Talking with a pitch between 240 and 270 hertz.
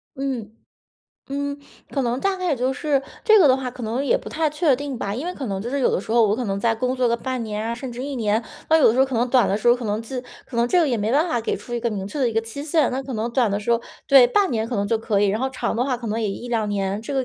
Yes: high, 245 Hz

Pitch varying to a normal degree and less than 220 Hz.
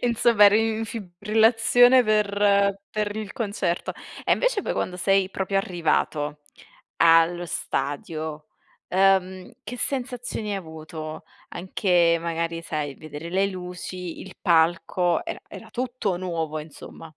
Yes: average, 4.1 semitones; medium, 185 Hz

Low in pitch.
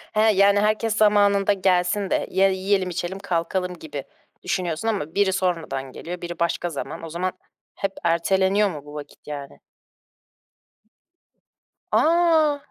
No: medium, 185 Hz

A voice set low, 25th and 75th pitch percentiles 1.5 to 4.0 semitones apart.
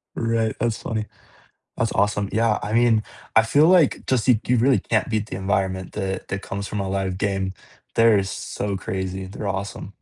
Yes: low, 105 Hz; average, 2.9 semitones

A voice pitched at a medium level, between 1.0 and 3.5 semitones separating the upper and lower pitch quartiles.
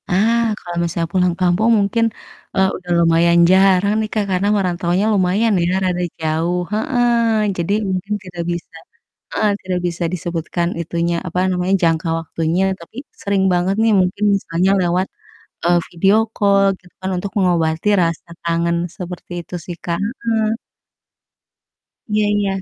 Yes: medium, 180 Hz; average, 2.8 semitones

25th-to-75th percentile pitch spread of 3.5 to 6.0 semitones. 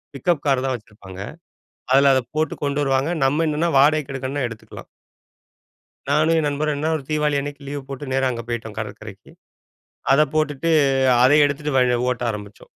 No: average, 2.7 semitones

